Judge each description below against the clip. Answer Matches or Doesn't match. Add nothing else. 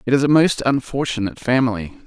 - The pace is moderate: Matches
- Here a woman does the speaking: Doesn't match